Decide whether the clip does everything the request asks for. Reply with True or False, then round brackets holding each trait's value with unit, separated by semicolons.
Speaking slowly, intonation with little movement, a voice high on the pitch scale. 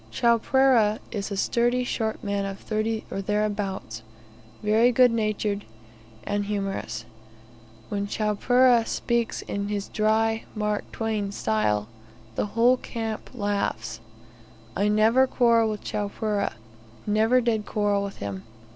True (120 wpm; 2.2 semitones; 210 Hz)